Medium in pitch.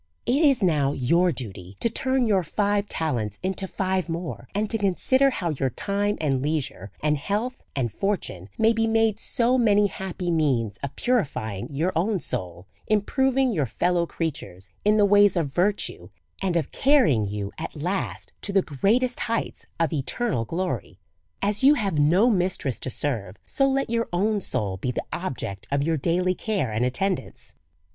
Yes: medium, 180 Hz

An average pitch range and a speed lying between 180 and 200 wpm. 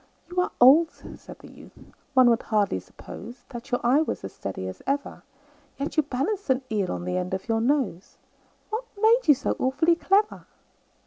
No: wide, 6.9 semitones; average, 190 wpm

